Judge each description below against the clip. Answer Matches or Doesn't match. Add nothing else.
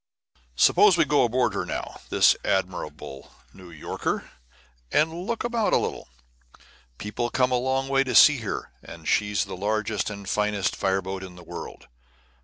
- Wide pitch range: Matches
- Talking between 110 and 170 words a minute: Matches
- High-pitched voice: Doesn't match